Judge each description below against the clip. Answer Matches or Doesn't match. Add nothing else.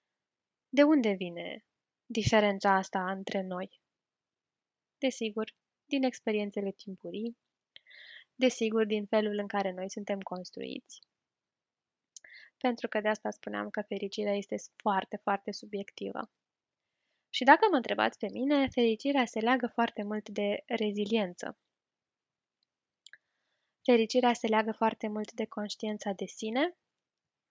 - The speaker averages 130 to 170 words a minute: Doesn't match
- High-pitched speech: Matches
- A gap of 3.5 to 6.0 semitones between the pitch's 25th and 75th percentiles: Doesn't match